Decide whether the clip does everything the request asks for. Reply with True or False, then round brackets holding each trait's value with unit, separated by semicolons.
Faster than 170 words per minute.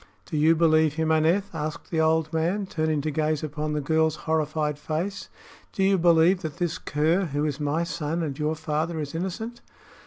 True (190 wpm)